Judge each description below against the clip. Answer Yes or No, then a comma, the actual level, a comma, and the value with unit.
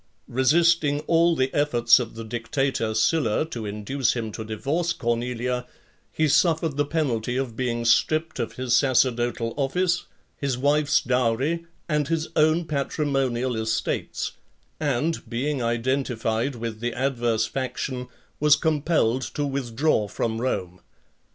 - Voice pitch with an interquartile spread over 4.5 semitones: No, average, 4.2 semitones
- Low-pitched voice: Yes, low, 130 Hz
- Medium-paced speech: No, slow, 130 wpm